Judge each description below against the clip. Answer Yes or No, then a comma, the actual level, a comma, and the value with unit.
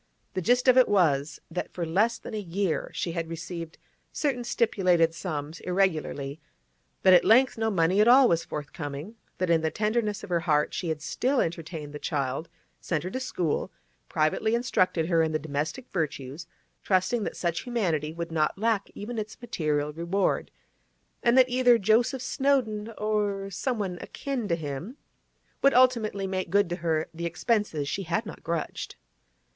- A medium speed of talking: Yes, average, 170 wpm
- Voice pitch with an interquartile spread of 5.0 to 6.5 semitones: Yes, wide, 5.5 semitones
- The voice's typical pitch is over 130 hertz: Yes, medium, 185 Hz